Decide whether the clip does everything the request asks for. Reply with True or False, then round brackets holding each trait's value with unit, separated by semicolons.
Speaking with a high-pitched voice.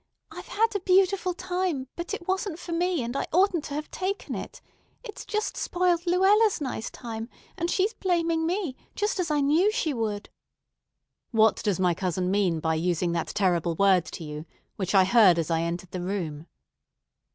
True (280 Hz)